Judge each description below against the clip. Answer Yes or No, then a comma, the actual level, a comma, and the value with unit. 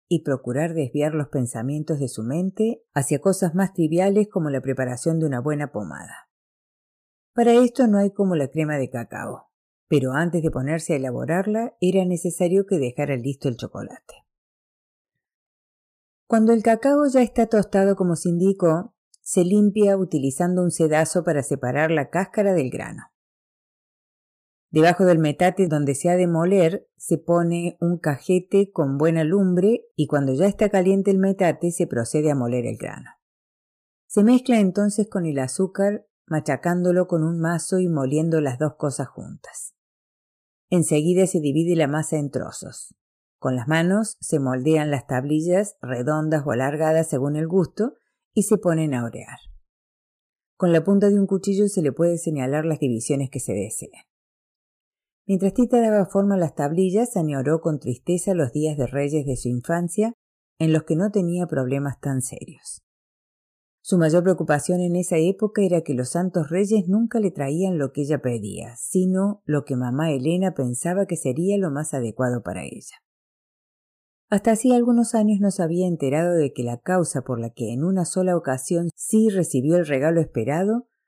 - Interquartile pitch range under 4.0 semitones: No, average, 5.1 semitones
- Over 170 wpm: No, average, 165 wpm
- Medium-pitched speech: Yes, medium, 165 Hz